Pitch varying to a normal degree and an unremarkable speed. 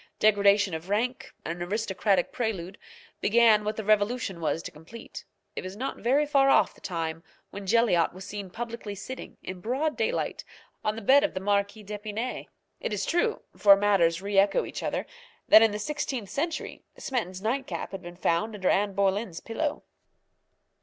Yes: average, 3.6 semitones; average, 175 wpm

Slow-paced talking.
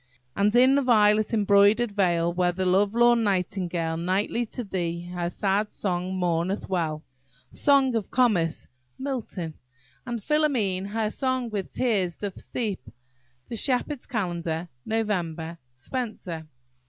Yes: slow, 125 wpm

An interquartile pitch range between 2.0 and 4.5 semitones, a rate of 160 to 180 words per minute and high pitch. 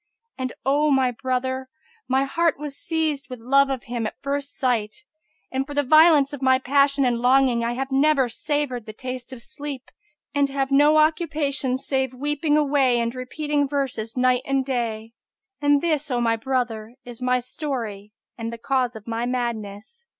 Yes: average, 2.9 semitones; average, 175 wpm; very high, 265 Hz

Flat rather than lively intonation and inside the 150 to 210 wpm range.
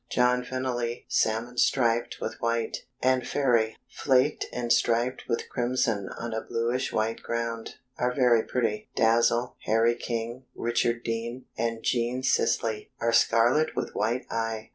No: narrow, 1.4 semitones; average, 140 wpm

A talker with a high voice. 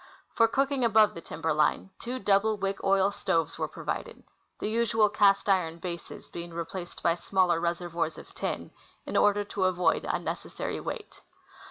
Yes: high, 195 Hz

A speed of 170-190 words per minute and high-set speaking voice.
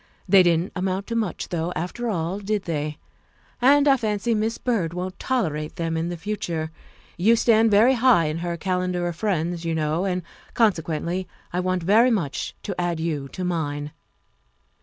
No: average, 180 wpm; medium, 180 Hz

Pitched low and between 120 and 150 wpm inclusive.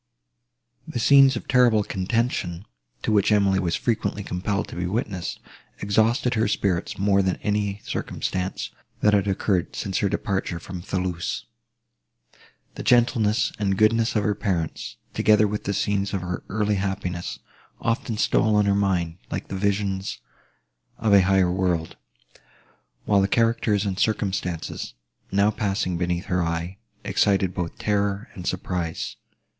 Yes: low, 100 Hz; average, 145 wpm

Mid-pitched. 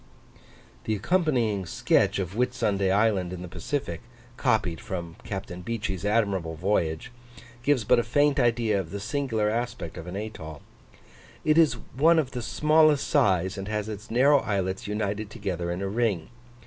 No: low, 105 Hz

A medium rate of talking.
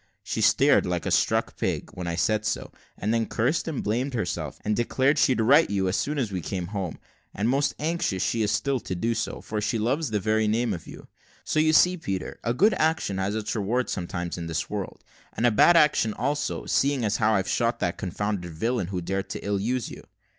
No: fast, 225 wpm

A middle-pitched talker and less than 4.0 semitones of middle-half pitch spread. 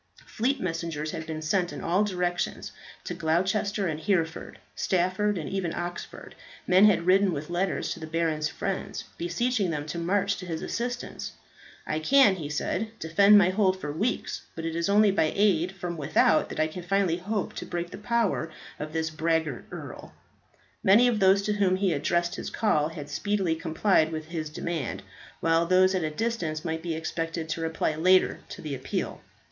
Yes: medium, 175 Hz; average, 3.6 semitones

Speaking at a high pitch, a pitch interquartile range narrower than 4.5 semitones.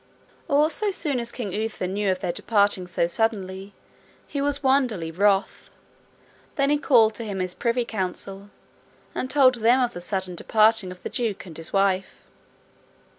No: high, 210 Hz; average, 4.8 semitones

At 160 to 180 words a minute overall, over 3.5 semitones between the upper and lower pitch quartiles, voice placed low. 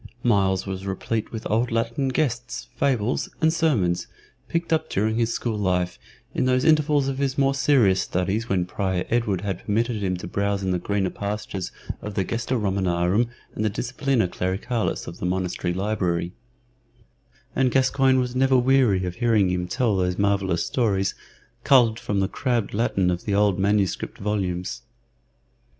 Yes: average, 165 wpm; average, 4.7 semitones; low, 105 Hz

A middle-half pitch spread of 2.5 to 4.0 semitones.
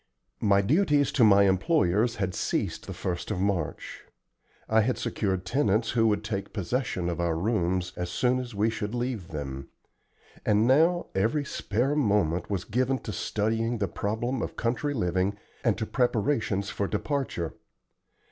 No: average, 4.5 semitones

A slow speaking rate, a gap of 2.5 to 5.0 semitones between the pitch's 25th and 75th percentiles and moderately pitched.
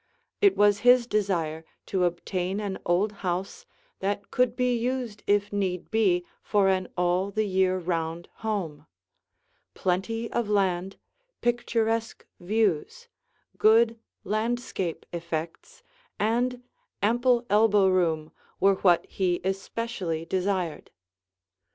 No: slow, 110 wpm; average, 4.0 semitones; high, 200 Hz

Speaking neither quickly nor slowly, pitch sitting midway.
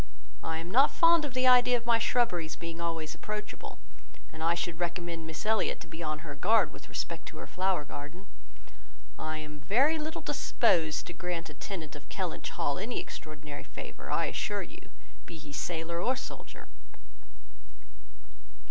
Yes: average, 170 wpm; medium, 170 Hz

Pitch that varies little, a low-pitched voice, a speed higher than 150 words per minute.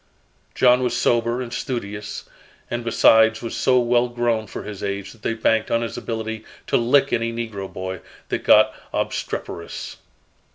Yes: narrow, 1.8 semitones; low, 115 Hz; average, 160 wpm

